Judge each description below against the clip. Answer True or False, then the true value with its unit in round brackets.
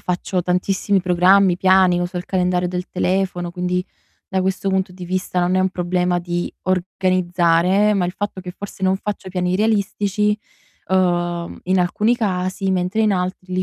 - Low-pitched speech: False (185 Hz)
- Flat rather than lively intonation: True (1.2 semitones)